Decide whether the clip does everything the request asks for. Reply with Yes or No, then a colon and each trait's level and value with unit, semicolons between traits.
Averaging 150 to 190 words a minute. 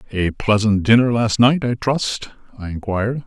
Yes: average, 165 wpm